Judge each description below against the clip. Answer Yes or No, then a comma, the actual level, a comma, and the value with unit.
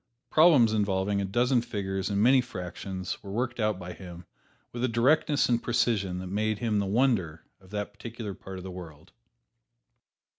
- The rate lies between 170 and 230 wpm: Yes, average, 175 wpm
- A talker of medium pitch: No, low, 105 Hz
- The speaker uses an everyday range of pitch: Yes, average, 4.1 semitones